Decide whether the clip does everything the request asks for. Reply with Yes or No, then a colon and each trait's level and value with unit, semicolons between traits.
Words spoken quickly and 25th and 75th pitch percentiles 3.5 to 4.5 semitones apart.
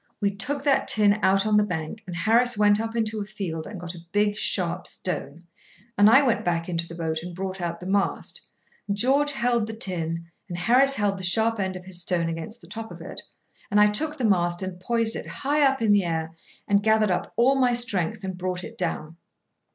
Yes: fast, 230 wpm; average, 4.2 semitones